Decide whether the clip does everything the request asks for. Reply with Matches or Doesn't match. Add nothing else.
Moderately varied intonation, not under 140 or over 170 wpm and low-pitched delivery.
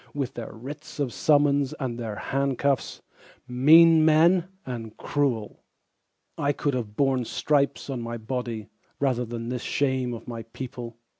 Matches